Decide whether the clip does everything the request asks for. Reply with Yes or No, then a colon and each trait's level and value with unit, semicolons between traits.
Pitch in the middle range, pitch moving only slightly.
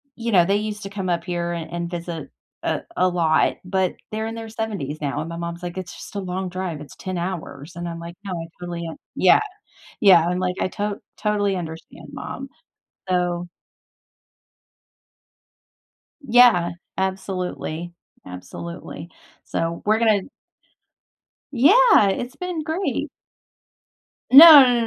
No: medium, 180 Hz; average, 3.7 semitones